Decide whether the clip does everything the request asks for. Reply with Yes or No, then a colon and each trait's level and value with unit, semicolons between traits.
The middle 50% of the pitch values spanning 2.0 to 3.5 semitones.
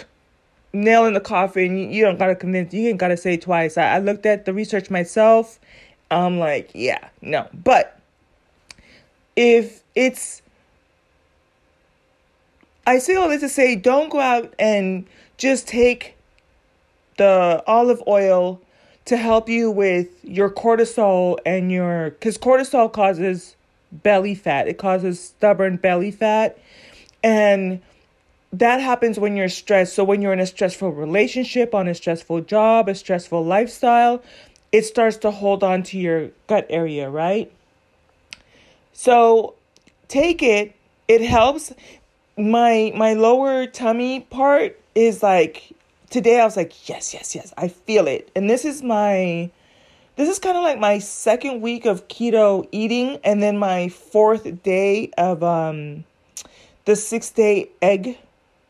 No: average, 4.0 semitones